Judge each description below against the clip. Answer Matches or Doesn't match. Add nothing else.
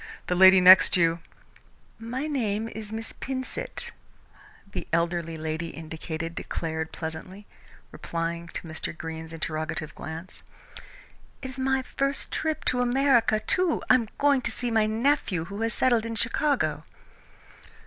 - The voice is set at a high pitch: Matches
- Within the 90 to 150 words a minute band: Matches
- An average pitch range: Doesn't match